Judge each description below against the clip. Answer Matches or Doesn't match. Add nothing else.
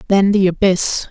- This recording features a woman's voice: Matches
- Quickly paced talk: Doesn't match